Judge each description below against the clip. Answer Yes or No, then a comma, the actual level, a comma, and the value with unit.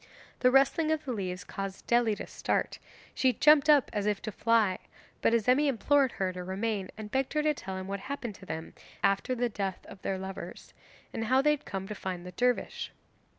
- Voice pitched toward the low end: No, high, 220 Hz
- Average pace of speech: No, fast, 210 wpm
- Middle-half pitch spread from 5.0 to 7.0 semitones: Yes, wide, 5.5 semitones